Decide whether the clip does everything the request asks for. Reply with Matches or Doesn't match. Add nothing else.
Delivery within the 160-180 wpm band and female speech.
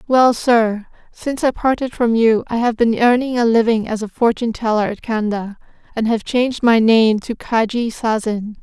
Doesn't match